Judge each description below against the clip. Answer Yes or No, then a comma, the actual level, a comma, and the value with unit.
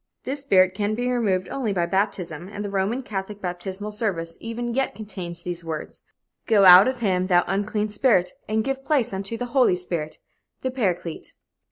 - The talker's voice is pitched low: No, high, 200 Hz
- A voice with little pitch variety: No, average, 4.3 semitones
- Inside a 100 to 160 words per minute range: No, average, 180 wpm